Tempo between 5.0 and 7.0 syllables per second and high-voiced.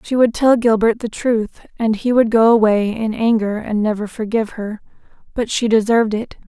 Yes: 5.1 syllables/s; high, 220 Hz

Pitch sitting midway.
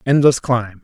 No: low, 125 Hz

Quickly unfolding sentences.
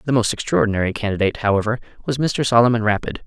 No: average, 165 wpm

